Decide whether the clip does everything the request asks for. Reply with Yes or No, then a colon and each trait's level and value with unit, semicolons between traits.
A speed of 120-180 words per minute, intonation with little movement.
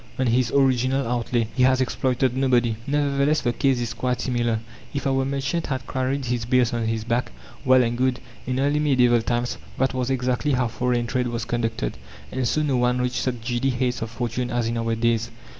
No: fast, 205 wpm; narrow, 1.8 semitones